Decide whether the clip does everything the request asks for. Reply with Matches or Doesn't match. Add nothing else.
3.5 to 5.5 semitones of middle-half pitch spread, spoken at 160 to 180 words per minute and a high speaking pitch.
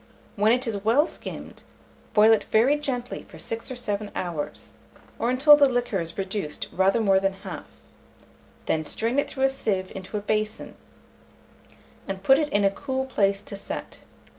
Matches